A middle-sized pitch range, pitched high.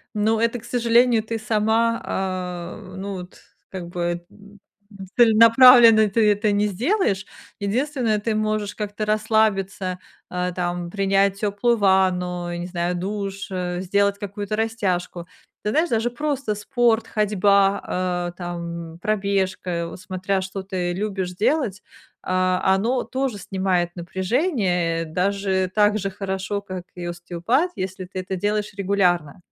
Yes: average, 3.0 semitones; high, 195 Hz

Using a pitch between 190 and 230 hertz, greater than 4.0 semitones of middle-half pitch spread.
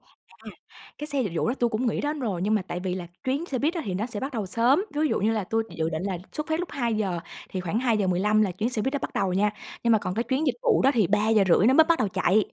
Yes: high, 220 Hz; wide, 5.6 semitones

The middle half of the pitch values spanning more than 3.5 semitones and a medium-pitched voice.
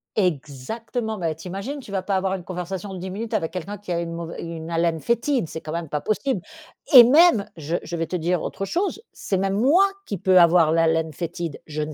Yes: average, 4.1 semitones; medium, 180 Hz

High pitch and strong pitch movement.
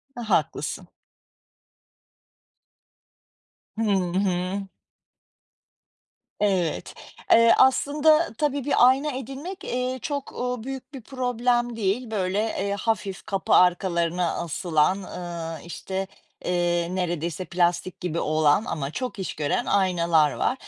Yes: high, 195 Hz; wide, 6.2 semitones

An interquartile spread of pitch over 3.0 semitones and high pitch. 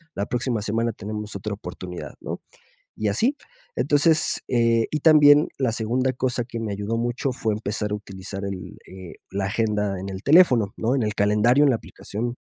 No: average, 3.6 semitones; low, 110 Hz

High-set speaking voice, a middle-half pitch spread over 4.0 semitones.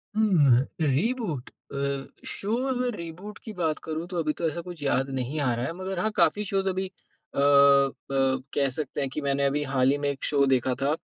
No: medium, 150 Hz; average, 5.0 semitones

